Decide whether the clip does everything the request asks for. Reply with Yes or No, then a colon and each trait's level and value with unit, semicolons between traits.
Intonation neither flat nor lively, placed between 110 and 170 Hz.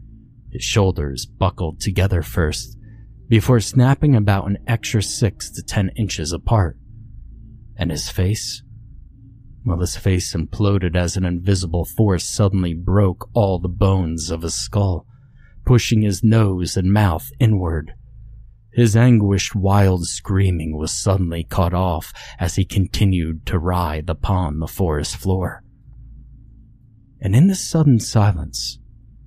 No: average, 4.2 semitones; low, 100 Hz